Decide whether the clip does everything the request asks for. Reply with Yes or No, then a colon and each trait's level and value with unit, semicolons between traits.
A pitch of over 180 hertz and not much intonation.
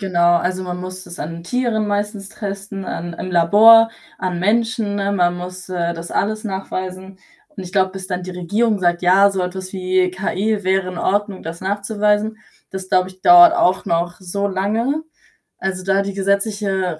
Yes: high, 190 Hz; narrow, 2.1 semitones